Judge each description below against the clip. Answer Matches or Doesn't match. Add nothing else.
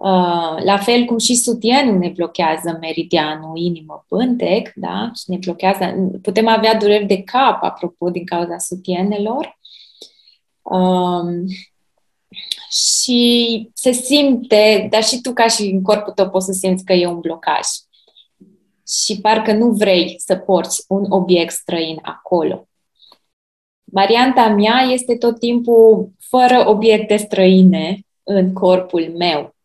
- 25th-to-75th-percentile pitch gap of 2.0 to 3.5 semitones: Doesn't match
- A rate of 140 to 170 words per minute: Doesn't match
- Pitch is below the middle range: Doesn't match